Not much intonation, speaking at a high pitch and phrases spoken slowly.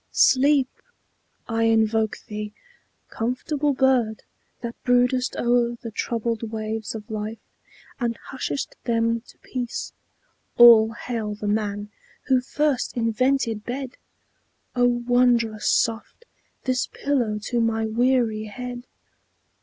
Yes: narrow, 2.3 semitones; high, 235 Hz; slow, 110 wpm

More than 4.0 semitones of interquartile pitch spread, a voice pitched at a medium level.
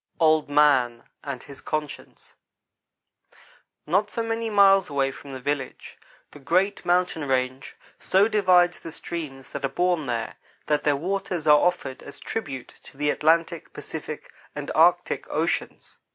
Yes: average, 4.7 semitones; medium, 155 Hz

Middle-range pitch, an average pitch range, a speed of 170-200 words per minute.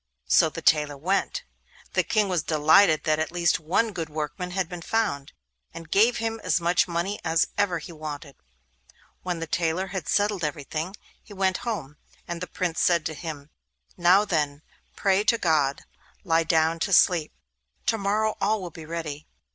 Yes: medium, 170 Hz; average, 3.7 semitones; average, 180 wpm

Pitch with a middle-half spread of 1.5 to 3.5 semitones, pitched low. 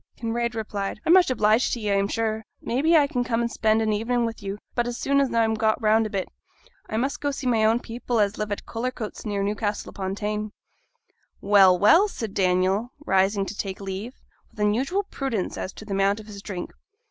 No: average, 3.0 semitones; high, 220 Hz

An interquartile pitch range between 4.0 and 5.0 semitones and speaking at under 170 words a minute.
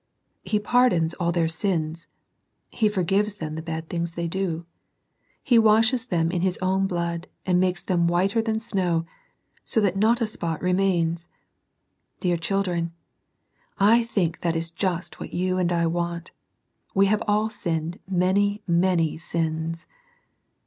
No: average, 3.1 semitones; average, 150 wpm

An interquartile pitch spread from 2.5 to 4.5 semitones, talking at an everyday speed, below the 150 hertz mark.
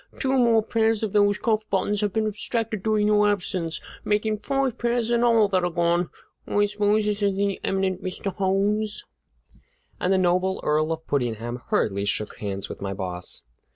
No: average, 3.7 semitones; average, 180 wpm; high, 205 Hz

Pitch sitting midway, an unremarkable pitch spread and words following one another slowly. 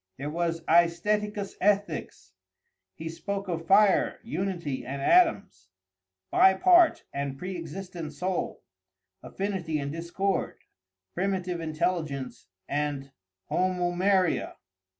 Yes: medium, 175 Hz; average, 3.8 semitones; slow, 95 wpm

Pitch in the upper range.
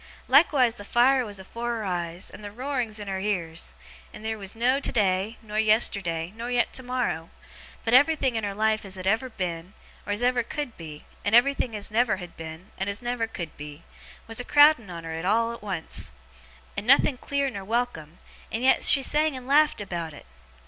Yes: high, 220 Hz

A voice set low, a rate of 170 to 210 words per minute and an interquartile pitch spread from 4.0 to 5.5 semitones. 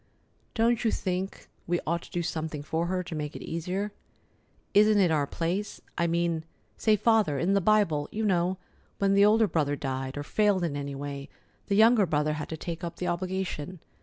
No: medium, 175 Hz; average, 195 wpm; average, 4.5 semitones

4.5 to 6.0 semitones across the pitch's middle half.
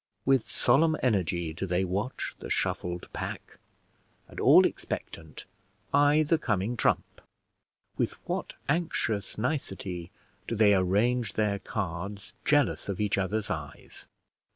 Yes: average, 5.2 semitones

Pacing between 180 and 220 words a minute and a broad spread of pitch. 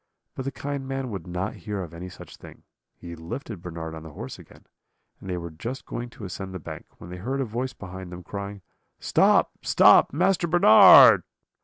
Yes: average, 200 wpm; wide, 6.5 semitones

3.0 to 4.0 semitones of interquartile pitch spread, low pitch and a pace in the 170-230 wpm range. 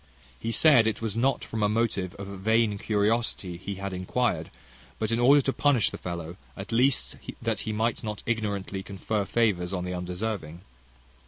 Yes: average, 3.3 semitones; low, 105 Hz; average, 175 wpm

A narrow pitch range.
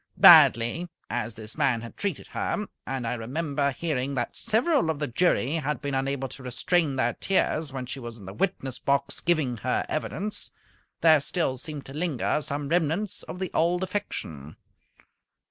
No: average, 5.0 semitones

